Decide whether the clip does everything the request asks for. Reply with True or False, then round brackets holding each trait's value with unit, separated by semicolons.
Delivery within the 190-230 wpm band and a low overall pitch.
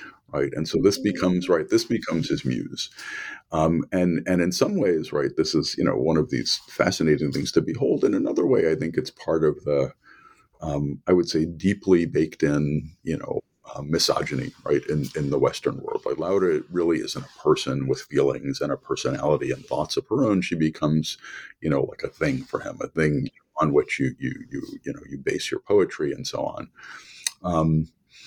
True (205 wpm; 90 Hz)